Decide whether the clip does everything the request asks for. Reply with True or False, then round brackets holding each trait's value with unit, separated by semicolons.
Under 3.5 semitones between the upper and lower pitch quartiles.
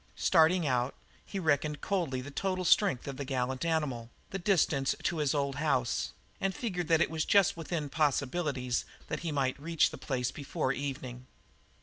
False (4.3 semitones)